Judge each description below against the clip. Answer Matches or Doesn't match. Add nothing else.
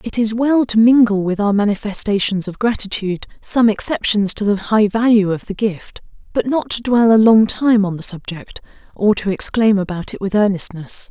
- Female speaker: Matches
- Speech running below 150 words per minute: Doesn't match